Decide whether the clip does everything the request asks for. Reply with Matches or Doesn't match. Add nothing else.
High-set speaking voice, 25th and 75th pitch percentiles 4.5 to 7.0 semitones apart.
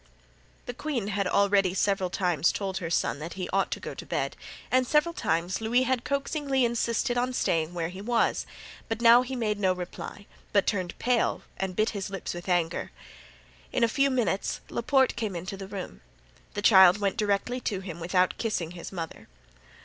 Matches